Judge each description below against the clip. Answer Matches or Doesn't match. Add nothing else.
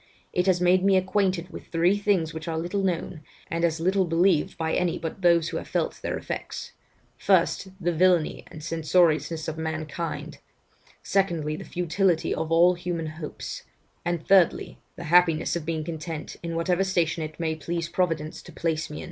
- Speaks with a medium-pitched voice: Matches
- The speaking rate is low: Doesn't match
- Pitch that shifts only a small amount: Matches